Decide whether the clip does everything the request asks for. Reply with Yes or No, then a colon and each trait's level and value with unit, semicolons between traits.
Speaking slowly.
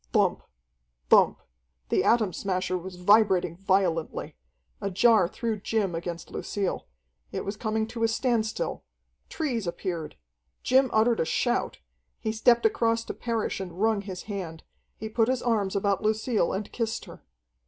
No: average, 150 wpm